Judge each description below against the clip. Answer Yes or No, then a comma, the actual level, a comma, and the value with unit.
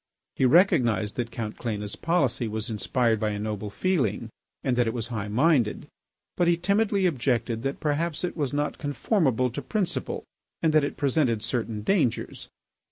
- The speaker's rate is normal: Yes, average, 165 wpm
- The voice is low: Yes, low, 125 Hz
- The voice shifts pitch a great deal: Yes, wide, 6.3 semitones